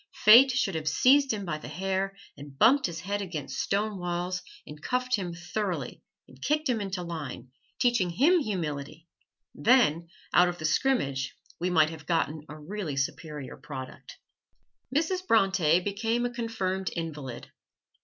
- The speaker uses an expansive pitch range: Yes, wide, 6.5 semitones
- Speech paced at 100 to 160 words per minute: Yes, average, 155 wpm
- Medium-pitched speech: Yes, medium, 180 Hz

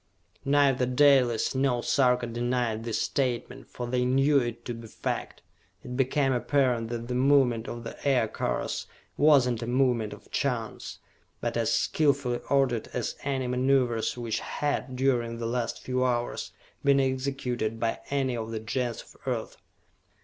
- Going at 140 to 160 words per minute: Yes, average, 155 wpm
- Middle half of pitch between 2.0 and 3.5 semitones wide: Yes, narrow, 2.4 semitones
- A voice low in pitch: Yes, low, 125 Hz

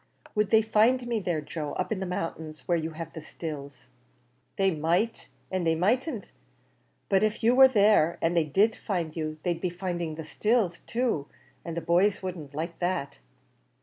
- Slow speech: No, average, 180 wpm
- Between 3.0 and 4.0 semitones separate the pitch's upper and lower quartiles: No, average, 4.8 semitones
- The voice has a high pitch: No, medium, 175 Hz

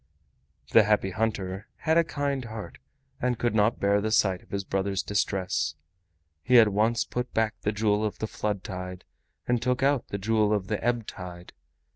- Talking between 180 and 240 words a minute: Yes, average, 185 wpm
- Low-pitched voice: Yes, low, 105 Hz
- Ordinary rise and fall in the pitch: Yes, average, 3.1 semitones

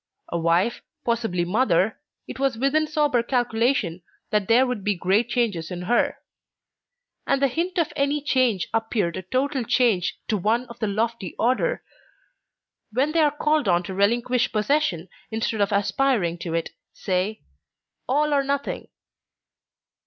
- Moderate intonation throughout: No, wide, 5.7 semitones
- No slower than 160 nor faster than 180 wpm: No, average, 150 wpm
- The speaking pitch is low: No, high, 230 Hz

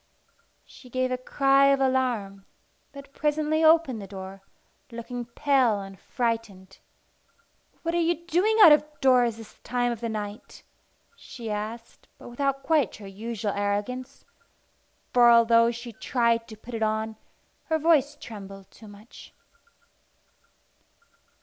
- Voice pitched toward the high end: Yes, high, 235 Hz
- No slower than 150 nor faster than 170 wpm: No, slow, 135 wpm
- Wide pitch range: No, average, 4.2 semitones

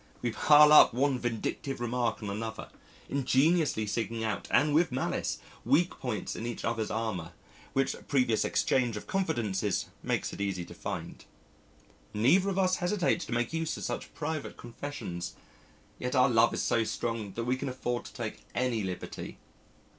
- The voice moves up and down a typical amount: Yes, average, 4.5 semitones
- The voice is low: Yes, low, 120 Hz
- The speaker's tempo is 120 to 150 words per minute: No, average, 165 wpm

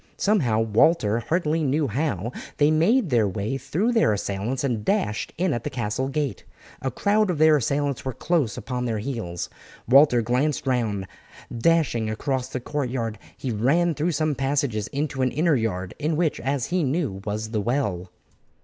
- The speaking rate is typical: Yes, average, 170 wpm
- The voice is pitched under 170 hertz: Yes, low, 135 Hz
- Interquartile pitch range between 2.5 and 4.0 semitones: No, wide, 5.5 semitones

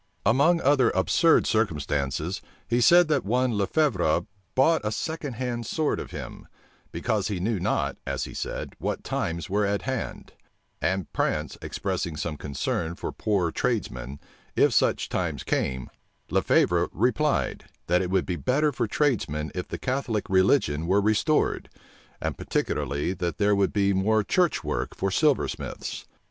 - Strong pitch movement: Yes, wide, 6.9 semitones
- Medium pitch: No, low, 100 Hz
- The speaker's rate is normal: Yes, average, 155 wpm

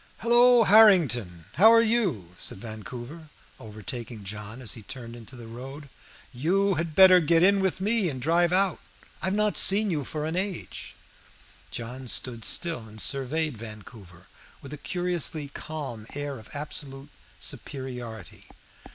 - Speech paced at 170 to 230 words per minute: No, average, 150 wpm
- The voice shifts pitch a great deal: Yes, wide, 7.5 semitones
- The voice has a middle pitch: Yes, medium, 145 Hz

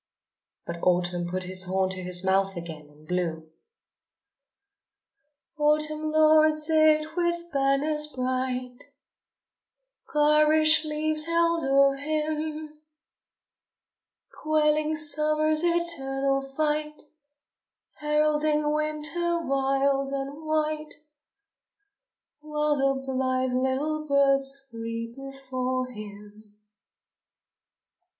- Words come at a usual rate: No, slow, 85 wpm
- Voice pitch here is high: Yes, very high, 285 Hz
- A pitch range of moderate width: Yes, average, 3.2 semitones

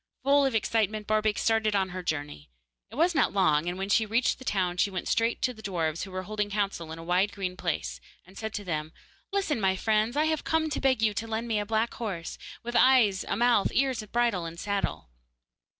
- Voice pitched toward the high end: Yes, high, 210 Hz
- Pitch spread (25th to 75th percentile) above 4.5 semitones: No, average, 3.9 semitones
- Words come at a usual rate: No, fast, 230 wpm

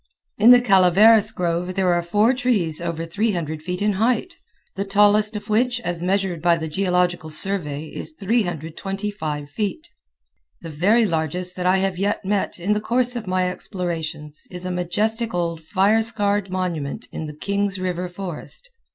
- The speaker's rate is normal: Yes, average, 165 wpm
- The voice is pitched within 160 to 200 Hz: Yes, medium, 185 Hz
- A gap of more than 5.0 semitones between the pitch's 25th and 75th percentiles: No, average, 3.4 semitones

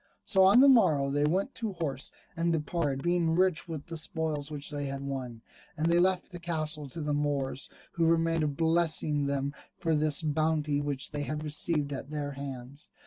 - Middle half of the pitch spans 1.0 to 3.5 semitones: Yes, average, 2.8 semitones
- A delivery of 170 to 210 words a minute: Yes, average, 190 wpm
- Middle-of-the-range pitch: Yes, medium, 150 Hz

